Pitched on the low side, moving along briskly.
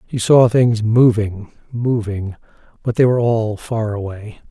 No: low, 110 Hz; average, 145 wpm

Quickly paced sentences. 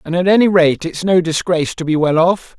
Yes: fast, 280 wpm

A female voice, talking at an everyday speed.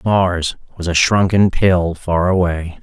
No: male; average, 150 wpm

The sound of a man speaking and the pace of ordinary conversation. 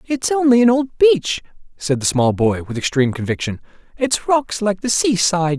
Yes: male; average, 185 wpm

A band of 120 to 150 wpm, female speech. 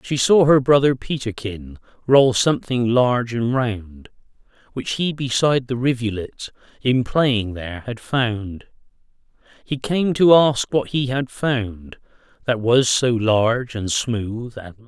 No: average, 145 wpm; male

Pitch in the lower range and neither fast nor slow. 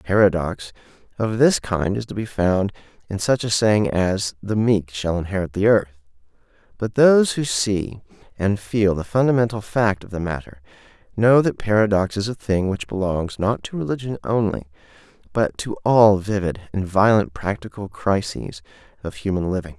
Yes: low, 100 Hz; average, 165 wpm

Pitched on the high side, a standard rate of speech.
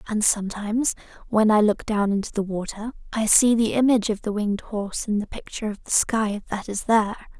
No: high, 215 Hz; fast, 210 wpm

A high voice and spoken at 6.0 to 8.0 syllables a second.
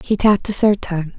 No: high, 195 Hz; 5.6 syllables/s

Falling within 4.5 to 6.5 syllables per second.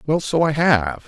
No: 4.3 syllables/s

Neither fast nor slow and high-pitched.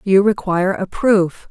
Yes: average, 160 wpm; high, 195 Hz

